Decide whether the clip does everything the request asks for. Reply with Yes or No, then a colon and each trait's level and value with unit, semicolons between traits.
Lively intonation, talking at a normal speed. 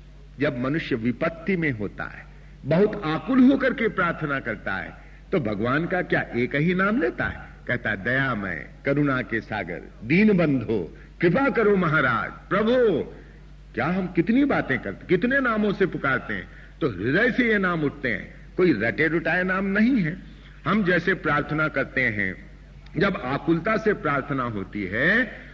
Yes: wide, 5.8 semitones; average, 160 wpm